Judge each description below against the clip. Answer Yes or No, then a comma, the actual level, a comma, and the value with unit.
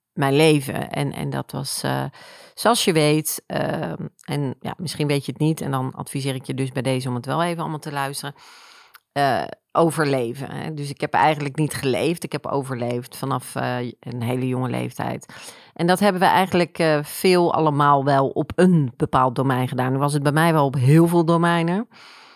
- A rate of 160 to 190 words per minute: No, fast, 200 wpm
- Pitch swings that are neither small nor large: Yes, average, 3.9 semitones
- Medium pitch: Yes, medium, 145 Hz